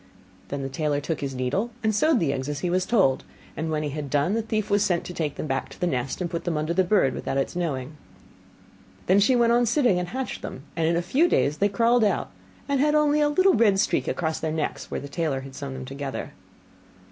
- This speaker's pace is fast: Yes, fast, 255 wpm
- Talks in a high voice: No, medium, 170 Hz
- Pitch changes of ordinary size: No, wide, 7.2 semitones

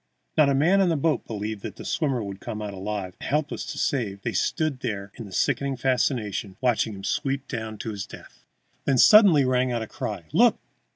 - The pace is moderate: No, fast, 210 wpm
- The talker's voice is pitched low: Yes, low, 120 Hz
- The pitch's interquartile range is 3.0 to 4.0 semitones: No, average, 5.1 semitones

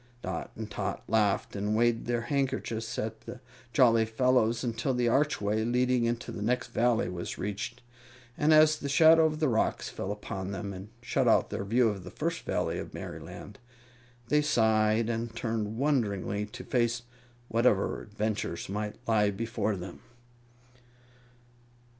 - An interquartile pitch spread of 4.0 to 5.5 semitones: No, average, 3.1 semitones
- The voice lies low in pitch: Yes, low, 115 Hz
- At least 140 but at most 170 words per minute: Yes, average, 155 wpm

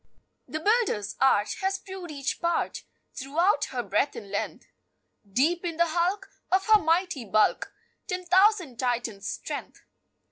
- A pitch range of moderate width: No, wide, 7.1 semitones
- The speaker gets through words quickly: No, average, 140 wpm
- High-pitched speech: Yes, very high, 330 Hz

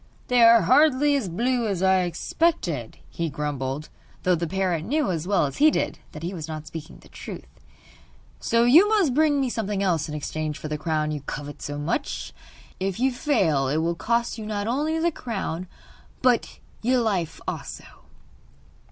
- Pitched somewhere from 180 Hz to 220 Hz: Yes, high, 190 Hz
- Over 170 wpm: Yes, average, 180 wpm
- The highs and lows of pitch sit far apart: Yes, wide, 8.0 semitones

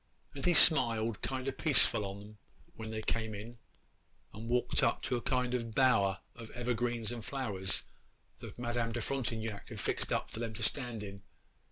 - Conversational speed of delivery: Yes, average, 180 wpm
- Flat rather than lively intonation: Yes, narrow, 2.1 semitones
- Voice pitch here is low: Yes, low, 115 Hz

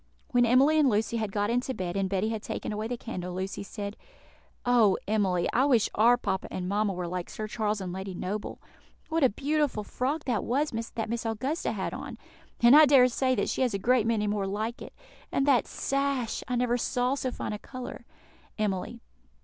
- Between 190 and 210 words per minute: Yes, fast, 205 wpm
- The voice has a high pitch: Yes, high, 225 Hz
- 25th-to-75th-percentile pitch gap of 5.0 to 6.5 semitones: No, average, 3.9 semitones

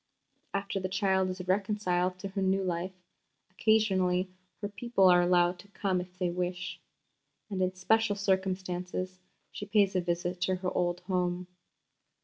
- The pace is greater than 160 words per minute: No, average, 150 wpm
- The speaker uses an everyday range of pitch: No, narrow, 1.4 semitones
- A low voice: No, medium, 185 Hz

